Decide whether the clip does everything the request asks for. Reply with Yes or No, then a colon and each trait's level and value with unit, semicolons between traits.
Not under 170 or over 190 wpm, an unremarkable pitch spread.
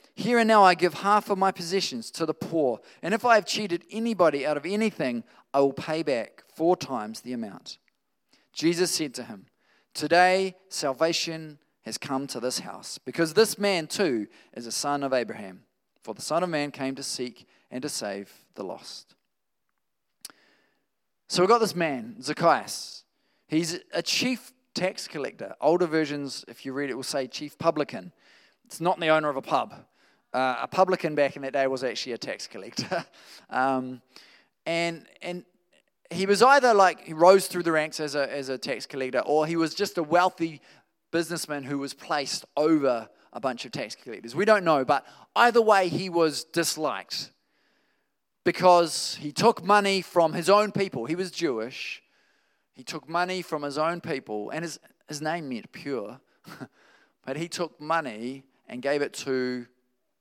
Yes: average, 175 wpm; average, 4.9 semitones